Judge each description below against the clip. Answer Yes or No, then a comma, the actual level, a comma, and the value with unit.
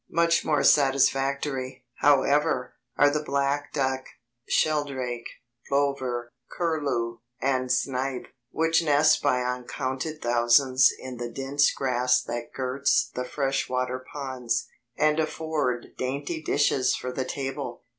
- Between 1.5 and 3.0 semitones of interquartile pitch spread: Yes, narrow, 2.4 semitones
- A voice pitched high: No, low, 135 Hz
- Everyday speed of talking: No, slow, 115 wpm